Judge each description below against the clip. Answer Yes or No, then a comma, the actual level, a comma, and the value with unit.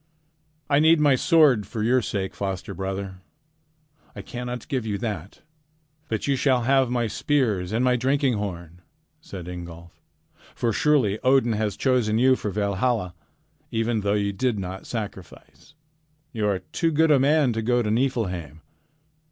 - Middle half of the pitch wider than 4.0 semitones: Yes, average, 4.7 semitones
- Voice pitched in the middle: No, low, 115 Hz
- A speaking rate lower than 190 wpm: Yes, average, 155 wpm